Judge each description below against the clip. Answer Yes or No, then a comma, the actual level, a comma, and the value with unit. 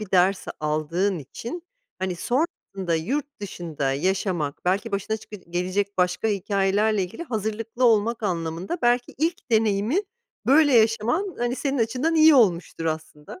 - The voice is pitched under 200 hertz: No, high, 205 Hz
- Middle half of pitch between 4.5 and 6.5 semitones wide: Yes, average, 5.1 semitones